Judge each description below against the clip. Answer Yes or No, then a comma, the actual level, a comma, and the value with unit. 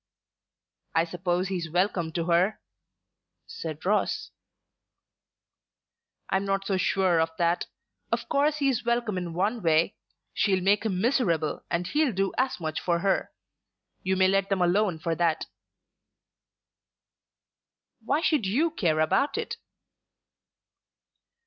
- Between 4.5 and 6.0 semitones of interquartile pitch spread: No, average, 3.9 semitones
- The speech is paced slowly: Yes, slow, 130 wpm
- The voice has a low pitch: No, high, 190 Hz